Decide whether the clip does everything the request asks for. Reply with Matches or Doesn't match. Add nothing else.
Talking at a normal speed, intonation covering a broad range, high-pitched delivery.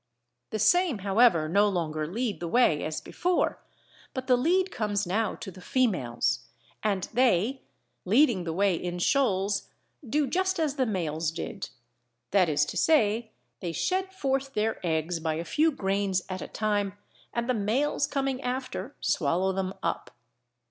Matches